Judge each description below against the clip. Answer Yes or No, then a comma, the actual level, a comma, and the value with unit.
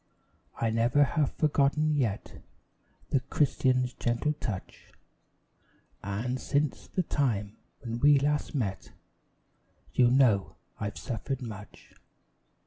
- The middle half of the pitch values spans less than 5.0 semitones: Yes, average, 4.3 semitones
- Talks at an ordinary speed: No, slow, 105 wpm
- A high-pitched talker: No, low, 125 Hz